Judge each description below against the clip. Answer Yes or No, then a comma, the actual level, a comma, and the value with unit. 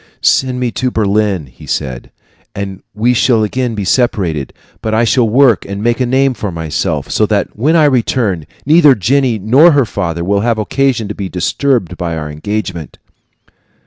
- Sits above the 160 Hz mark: No, low, 110 Hz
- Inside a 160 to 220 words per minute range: Yes, average, 175 wpm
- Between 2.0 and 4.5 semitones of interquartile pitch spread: No, average, 5.3 semitones